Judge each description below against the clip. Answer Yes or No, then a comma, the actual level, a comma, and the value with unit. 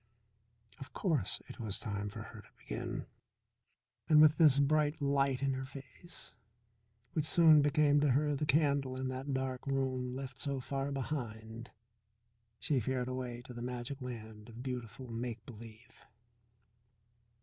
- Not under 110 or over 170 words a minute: Yes, average, 150 wpm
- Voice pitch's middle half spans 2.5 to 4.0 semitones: Yes, average, 2.8 semitones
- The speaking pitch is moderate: No, low, 130 Hz